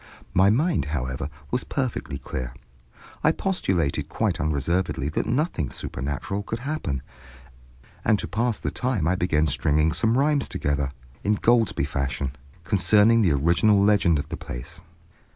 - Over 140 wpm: No, slow, 135 wpm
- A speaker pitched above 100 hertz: No, very low, 90 Hz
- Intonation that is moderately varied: No, wide, 7.9 semitones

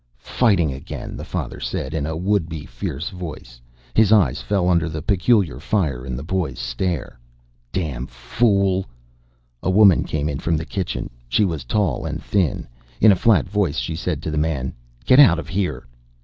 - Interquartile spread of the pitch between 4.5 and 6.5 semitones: Yes, wide, 5.5 semitones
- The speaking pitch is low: Yes, very low, 85 Hz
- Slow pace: No, average, 185 wpm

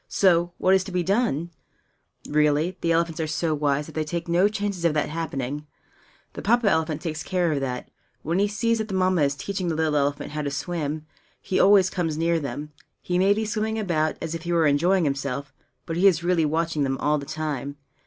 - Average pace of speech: No, fast, 220 wpm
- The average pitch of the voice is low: No, medium, 165 Hz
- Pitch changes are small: No, average, 3.5 semitones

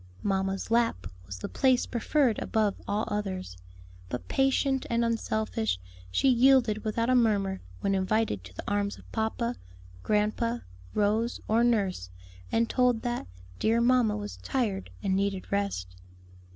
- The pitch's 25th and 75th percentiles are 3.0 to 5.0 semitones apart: Yes, average, 3.3 semitones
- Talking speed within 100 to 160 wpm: Yes, average, 140 wpm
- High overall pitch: Yes, high, 215 Hz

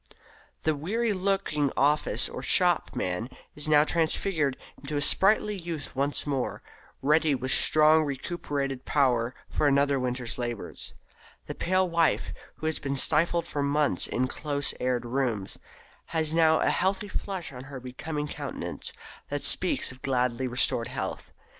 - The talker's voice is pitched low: No, medium, 145 Hz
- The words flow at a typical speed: Yes, average, 145 wpm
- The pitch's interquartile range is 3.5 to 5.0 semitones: Yes, average, 3.8 semitones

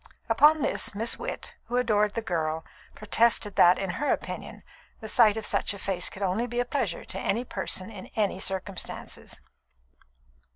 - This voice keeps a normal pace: Yes, average, 175 wpm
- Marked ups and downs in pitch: No, average, 3.7 semitones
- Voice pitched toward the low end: No, high, 210 Hz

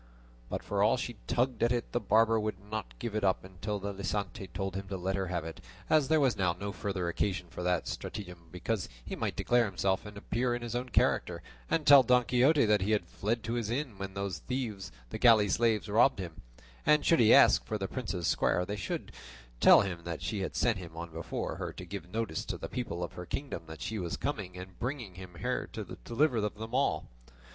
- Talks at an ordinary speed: No, fast, 230 wpm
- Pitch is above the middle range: No, low, 100 Hz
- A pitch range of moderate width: Yes, average, 4.4 semitones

